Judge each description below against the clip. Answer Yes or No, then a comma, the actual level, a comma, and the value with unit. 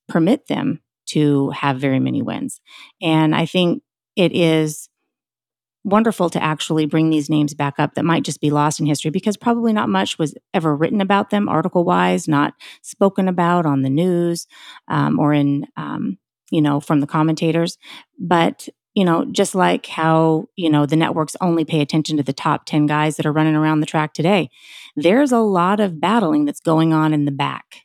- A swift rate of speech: No, average, 190 wpm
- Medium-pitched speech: Yes, medium, 160 Hz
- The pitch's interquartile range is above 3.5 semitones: No, average, 3.1 semitones